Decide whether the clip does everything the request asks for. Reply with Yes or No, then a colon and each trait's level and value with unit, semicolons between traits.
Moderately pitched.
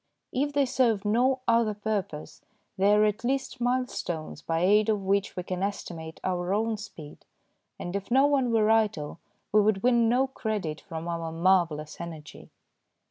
No: high, 205 Hz